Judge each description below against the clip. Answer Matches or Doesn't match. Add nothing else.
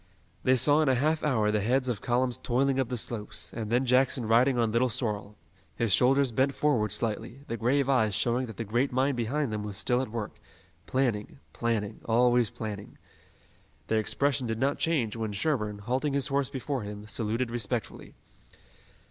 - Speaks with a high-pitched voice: Doesn't match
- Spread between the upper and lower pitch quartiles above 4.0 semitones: Doesn't match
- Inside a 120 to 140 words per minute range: Doesn't match